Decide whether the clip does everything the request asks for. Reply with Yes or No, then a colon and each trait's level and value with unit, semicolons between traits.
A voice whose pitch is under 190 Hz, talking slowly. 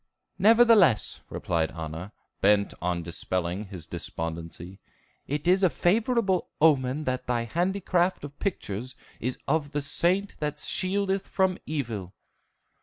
Yes: medium, 140 Hz; slow, 120 wpm